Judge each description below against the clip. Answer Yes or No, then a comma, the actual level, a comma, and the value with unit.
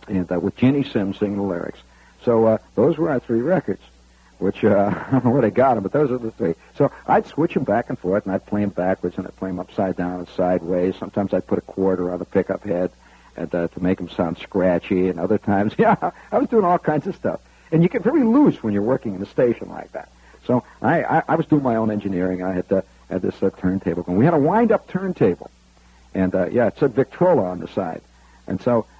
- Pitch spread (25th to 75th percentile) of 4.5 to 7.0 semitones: Yes, average, 5.1 semitones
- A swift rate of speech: Yes, fast, 255 wpm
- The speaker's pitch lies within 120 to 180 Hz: No, very low, 95 Hz